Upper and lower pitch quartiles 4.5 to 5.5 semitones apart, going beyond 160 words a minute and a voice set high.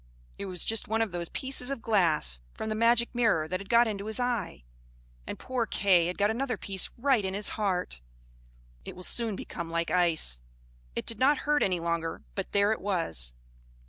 Yes: average, 5.1 semitones; average, 200 wpm; high, 200 Hz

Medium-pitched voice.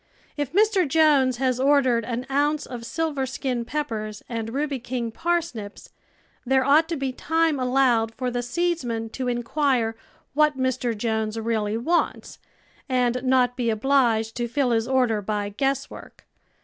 No: very high, 255 Hz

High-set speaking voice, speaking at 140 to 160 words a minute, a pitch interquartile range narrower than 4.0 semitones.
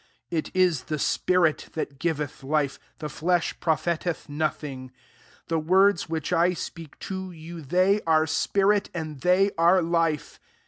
No: medium, 165 Hz; average, 145 wpm; average, 2.8 semitones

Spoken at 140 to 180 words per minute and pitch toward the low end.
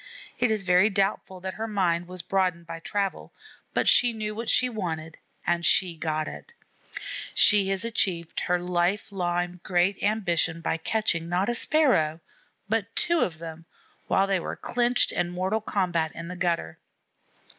No: average, 165 wpm; medium, 185 Hz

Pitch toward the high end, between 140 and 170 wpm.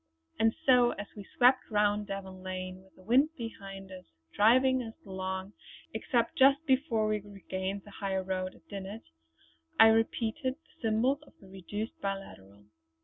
Yes: high, 205 Hz; average, 155 wpm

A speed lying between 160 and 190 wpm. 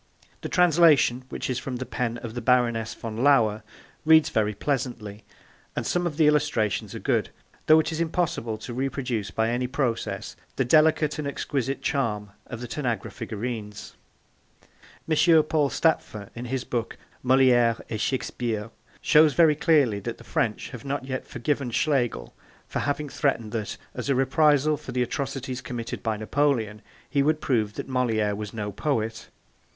Yes: average, 165 wpm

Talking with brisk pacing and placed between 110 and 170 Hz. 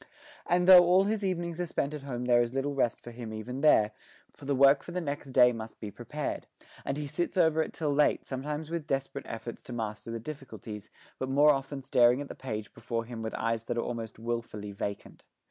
Yes: fast, 225 wpm; low, 135 Hz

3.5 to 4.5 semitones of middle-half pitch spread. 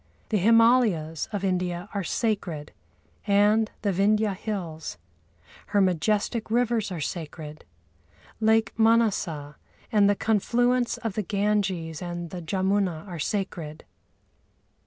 Yes: average, 4.1 semitones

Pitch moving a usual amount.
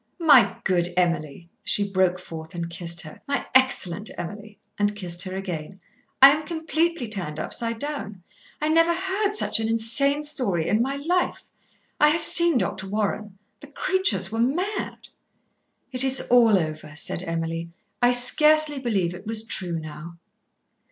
No: wide, 8.5 semitones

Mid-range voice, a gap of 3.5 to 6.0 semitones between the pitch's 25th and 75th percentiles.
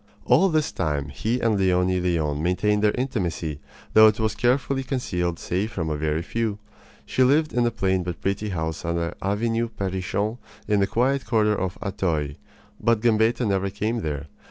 No: low, 100 Hz; average, 4.8 semitones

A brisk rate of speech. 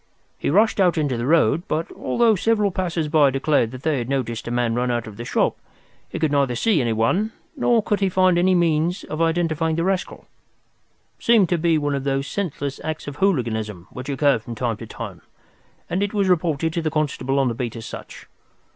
Yes: fast, 215 wpm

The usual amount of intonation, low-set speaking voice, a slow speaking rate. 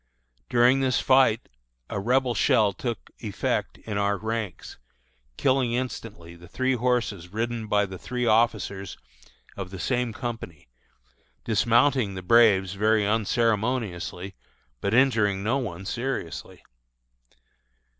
Yes: average, 3.7 semitones; low, 110 Hz; slow, 115 wpm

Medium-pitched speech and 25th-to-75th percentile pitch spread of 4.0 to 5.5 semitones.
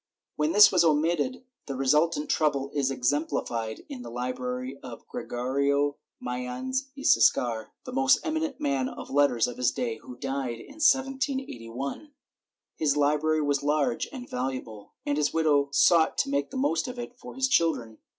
Yes: medium, 145 Hz; average, 5.0 semitones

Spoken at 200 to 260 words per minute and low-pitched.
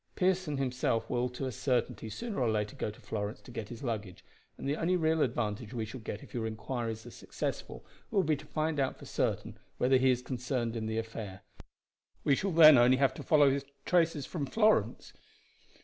Yes: fast, 205 wpm; low, 125 Hz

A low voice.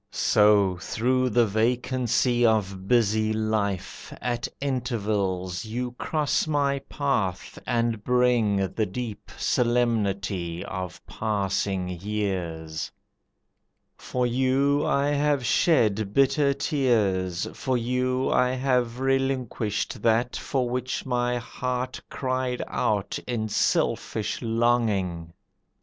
Yes: low, 115 Hz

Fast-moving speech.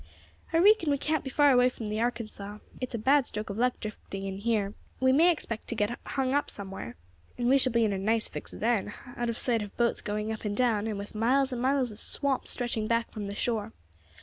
Yes: fast, 240 wpm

